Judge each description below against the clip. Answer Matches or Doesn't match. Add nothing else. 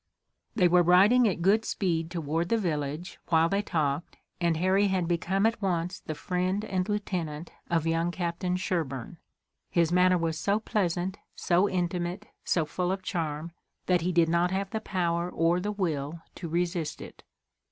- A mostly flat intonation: Matches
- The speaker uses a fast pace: Doesn't match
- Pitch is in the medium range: Matches